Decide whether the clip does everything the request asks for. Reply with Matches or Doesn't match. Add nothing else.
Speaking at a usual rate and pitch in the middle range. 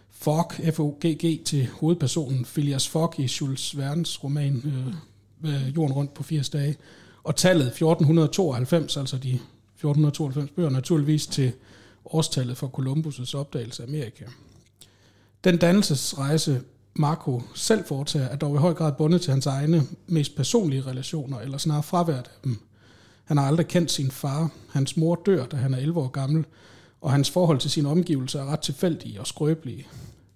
Matches